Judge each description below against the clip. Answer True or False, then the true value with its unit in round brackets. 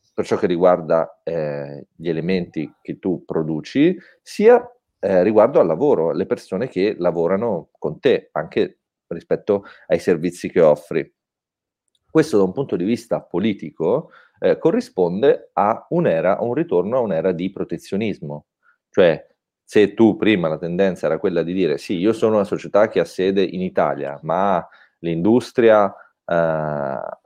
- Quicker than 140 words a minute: True (150 wpm)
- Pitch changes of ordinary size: False (7.6 semitones)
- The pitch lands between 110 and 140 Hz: False (95 Hz)